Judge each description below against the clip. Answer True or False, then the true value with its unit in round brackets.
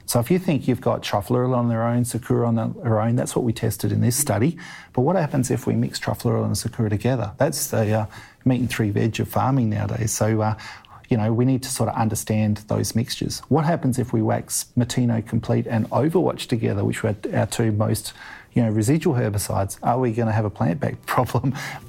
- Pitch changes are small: True (2.3 semitones)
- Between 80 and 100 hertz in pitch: False (115 Hz)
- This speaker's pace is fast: True (220 wpm)